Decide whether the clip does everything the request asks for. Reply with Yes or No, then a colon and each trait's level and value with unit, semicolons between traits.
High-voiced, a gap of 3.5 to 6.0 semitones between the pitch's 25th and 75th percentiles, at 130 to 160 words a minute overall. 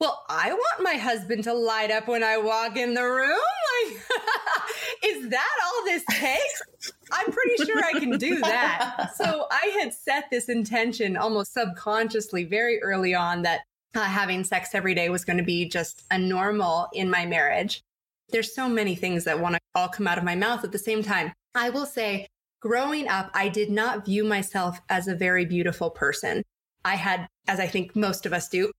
No: high, 215 Hz; average, 4.7 semitones; average, 200 wpm